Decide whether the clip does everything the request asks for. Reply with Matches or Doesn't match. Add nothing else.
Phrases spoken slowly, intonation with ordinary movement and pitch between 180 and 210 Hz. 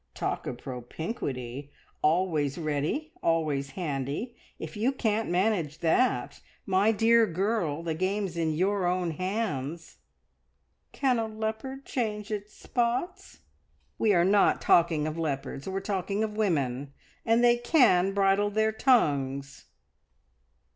Doesn't match